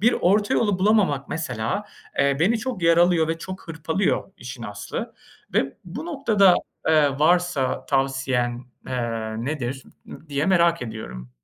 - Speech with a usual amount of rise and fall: No, wide, 6.0 semitones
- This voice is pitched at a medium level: Yes, medium, 160 Hz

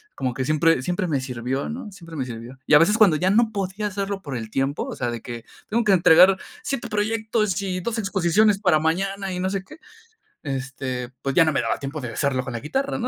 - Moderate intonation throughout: No, wide, 6.9 semitones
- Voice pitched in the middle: Yes, medium, 175 Hz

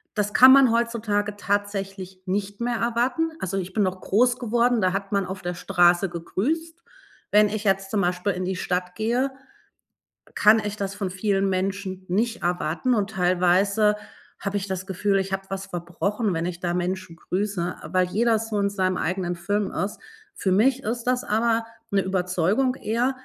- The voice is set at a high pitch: Yes, high, 200 Hz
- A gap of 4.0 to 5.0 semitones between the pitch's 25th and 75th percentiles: No, average, 3.1 semitones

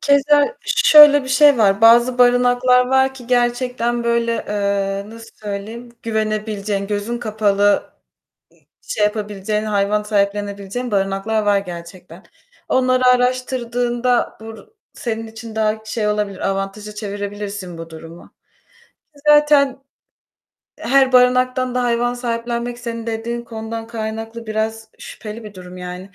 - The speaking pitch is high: Yes, high, 225 Hz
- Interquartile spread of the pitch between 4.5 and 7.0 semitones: No, average, 3.2 semitones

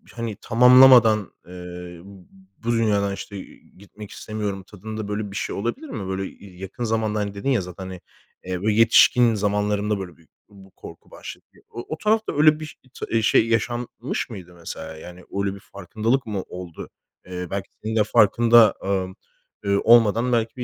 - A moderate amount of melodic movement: Yes, average, 3.1 semitones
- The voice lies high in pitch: No, low, 105 Hz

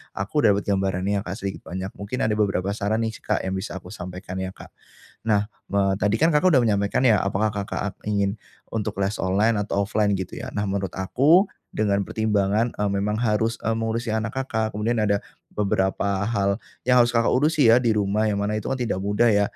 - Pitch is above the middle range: No, low, 105 Hz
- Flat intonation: Yes, narrow, 2.3 semitones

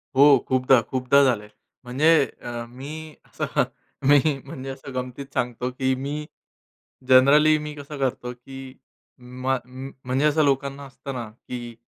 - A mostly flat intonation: Yes, narrow, 1.9 semitones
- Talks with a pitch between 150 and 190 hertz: No, low, 135 Hz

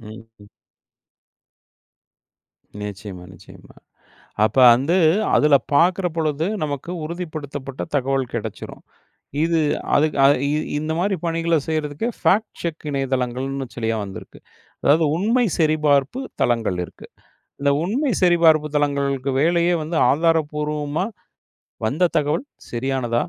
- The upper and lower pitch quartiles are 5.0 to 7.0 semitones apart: No, average, 3.7 semitones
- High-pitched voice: No, medium, 150 Hz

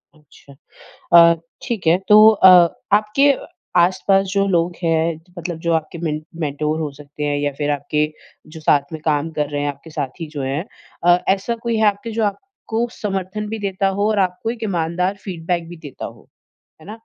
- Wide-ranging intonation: No, average, 4.8 semitones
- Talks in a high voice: No, medium, 170 Hz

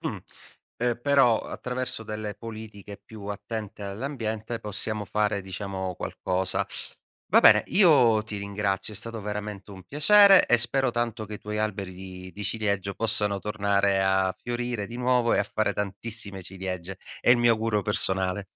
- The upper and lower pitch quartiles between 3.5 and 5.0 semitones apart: No, average, 2.7 semitones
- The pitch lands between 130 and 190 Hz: No, low, 105 Hz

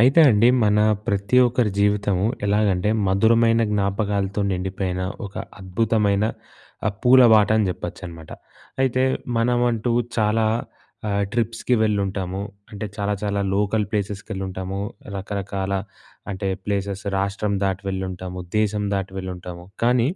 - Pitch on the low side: Yes, low, 100 Hz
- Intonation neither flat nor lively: No, narrow, 2.2 semitones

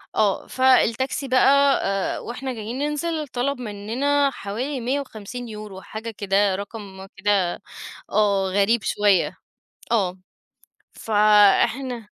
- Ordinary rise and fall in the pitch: Yes, average, 4.4 semitones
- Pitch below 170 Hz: No, high, 220 Hz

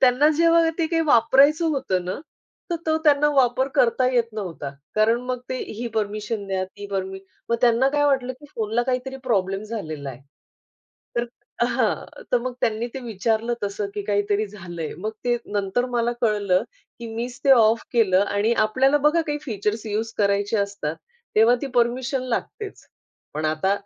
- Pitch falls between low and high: No, high, 230 Hz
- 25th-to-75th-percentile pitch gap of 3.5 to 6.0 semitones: Yes, average, 4.1 semitones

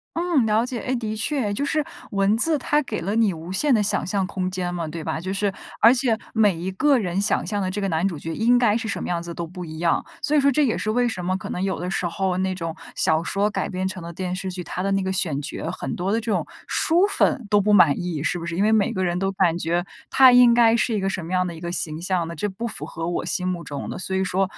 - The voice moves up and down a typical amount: Yes, average, 4.0 semitones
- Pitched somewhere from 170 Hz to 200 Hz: Yes, high, 190 Hz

